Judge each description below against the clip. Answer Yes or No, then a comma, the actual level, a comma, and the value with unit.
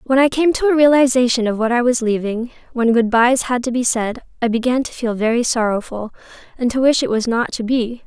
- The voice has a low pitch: No, high, 240 Hz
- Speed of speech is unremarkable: No, fast, 240 wpm